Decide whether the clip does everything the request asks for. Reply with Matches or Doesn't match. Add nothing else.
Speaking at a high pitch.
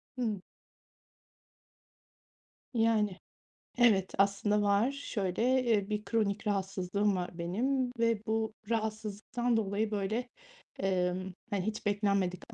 Matches